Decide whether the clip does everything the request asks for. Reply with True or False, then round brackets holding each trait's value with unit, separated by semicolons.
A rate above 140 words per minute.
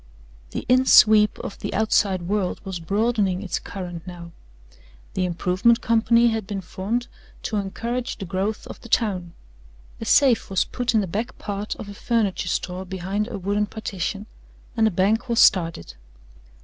True (170 wpm)